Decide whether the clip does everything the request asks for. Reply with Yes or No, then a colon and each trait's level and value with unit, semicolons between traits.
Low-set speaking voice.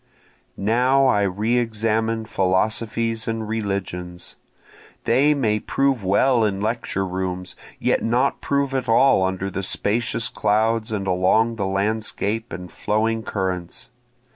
Yes: low, 110 Hz